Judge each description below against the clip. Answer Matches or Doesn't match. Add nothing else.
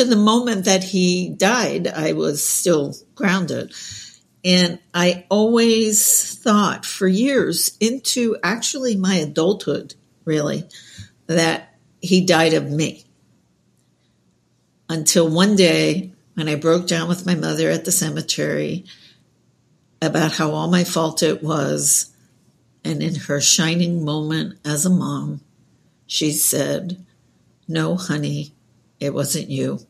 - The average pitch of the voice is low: Doesn't match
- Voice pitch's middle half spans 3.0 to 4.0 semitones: Matches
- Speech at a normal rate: Doesn't match